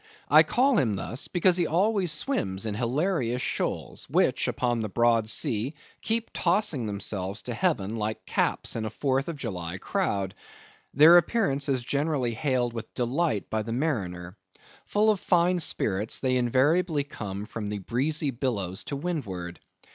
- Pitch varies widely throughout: Yes, wide, 7.2 semitones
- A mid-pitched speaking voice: No, low, 125 Hz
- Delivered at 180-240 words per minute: No, average, 155 wpm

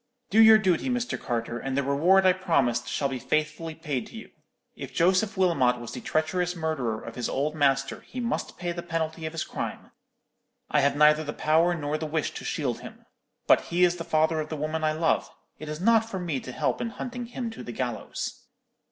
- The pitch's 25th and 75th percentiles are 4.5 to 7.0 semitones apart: No, average, 4.1 semitones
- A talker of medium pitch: Yes, medium, 160 Hz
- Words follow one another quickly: Yes, fast, 220 wpm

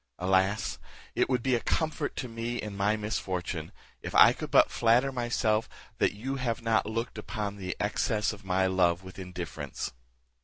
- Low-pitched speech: Yes, low, 105 Hz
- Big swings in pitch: No, average, 3.7 semitones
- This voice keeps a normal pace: Yes, average, 170 wpm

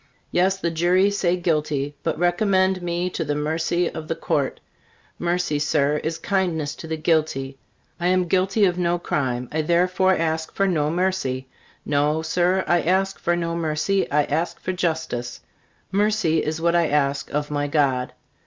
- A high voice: No, medium, 165 Hz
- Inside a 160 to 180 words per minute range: Yes, average, 170 wpm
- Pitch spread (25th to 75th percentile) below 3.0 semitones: No, average, 3.3 semitones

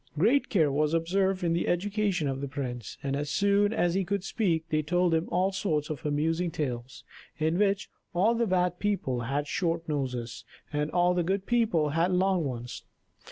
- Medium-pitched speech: Yes, medium, 170 Hz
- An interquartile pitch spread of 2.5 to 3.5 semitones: No, average, 4.6 semitones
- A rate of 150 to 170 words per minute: No, average, 190 wpm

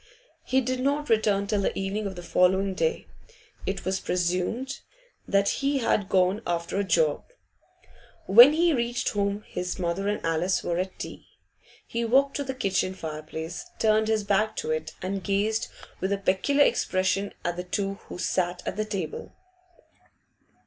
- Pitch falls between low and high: No, high, 195 Hz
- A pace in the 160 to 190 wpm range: Yes, average, 165 wpm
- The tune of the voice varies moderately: Yes, average, 3.5 semitones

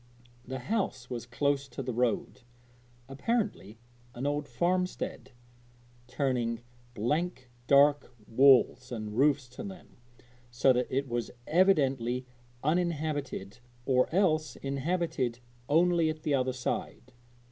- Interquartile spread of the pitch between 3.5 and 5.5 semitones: Yes, average, 4.0 semitones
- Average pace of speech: No, slow, 115 wpm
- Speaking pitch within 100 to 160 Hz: Yes, low, 135 Hz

